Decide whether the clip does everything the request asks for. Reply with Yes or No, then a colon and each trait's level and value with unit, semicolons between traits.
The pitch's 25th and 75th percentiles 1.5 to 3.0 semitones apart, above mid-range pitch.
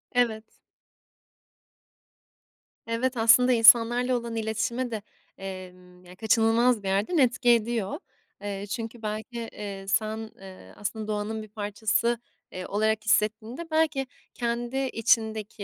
Yes: narrow, 2.5 semitones; high, 220 Hz